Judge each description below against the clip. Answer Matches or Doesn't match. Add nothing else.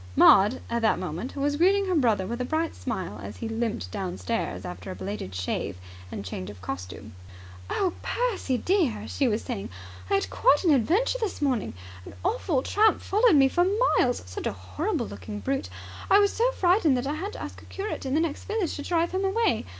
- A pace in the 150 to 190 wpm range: Doesn't match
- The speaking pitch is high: Matches